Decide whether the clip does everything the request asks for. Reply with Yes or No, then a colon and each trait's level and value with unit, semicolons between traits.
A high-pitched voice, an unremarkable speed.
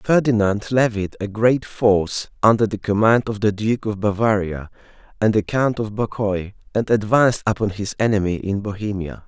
No: low, 105 Hz; average, 160 wpm